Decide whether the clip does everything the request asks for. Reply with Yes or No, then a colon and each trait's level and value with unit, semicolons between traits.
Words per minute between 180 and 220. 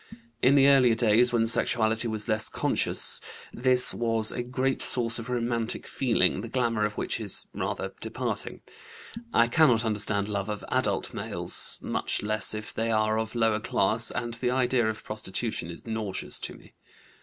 No: average, 165 wpm